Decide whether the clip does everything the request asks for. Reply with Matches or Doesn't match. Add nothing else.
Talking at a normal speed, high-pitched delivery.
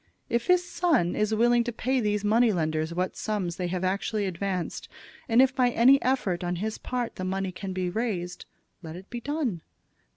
Matches